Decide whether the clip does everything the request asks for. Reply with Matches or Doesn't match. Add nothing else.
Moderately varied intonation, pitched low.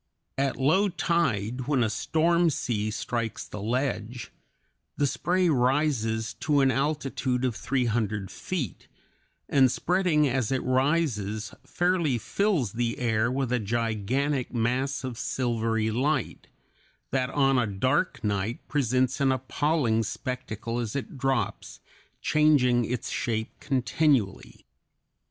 Matches